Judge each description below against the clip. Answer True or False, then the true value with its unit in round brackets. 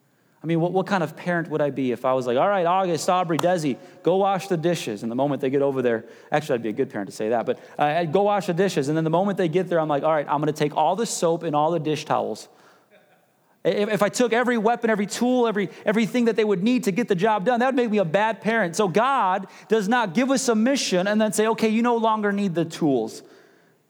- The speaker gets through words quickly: True (285 wpm)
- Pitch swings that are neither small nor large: False (6.3 semitones)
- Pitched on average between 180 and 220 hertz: True (190 Hz)